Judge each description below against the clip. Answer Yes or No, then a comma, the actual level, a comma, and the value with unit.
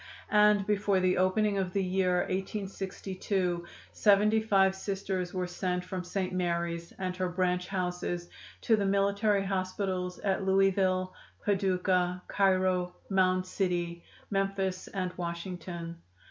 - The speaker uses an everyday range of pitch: No, narrow, 1.5 semitones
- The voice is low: No, medium, 185 Hz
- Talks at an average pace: No, slow, 120 wpm